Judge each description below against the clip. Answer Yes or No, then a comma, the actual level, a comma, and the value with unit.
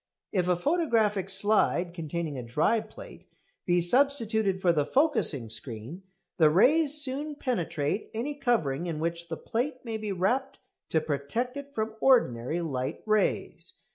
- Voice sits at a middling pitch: No, high, 195 Hz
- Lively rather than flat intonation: Yes, wide, 7.7 semitones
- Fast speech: No, average, 145 wpm